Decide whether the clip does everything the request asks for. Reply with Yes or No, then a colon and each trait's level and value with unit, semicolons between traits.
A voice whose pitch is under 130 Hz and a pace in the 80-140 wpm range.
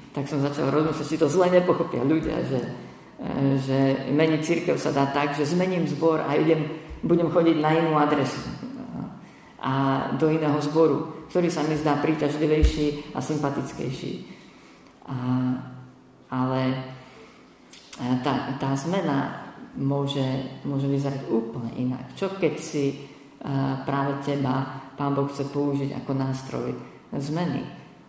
No: medium, 140 Hz; average, 130 wpm